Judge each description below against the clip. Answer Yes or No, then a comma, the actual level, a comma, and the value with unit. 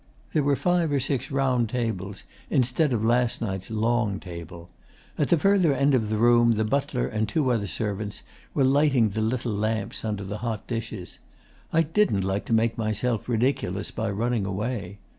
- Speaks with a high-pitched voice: No, low, 115 Hz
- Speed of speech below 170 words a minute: No, average, 180 wpm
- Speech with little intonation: No, average, 3.7 semitones